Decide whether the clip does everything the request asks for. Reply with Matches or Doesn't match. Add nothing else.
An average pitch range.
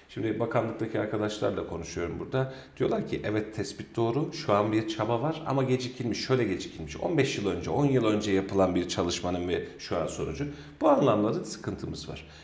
Matches